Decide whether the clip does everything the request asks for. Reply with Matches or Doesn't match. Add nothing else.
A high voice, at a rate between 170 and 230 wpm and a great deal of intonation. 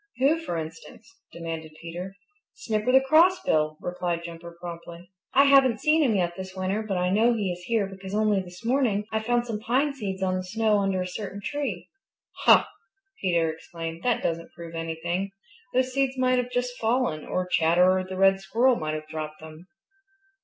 Matches